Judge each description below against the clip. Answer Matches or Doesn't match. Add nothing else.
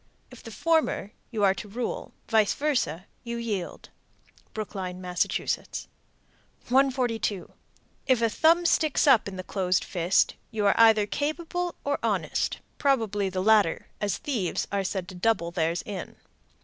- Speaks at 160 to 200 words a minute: Doesn't match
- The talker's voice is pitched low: Doesn't match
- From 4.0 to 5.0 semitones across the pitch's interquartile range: Doesn't match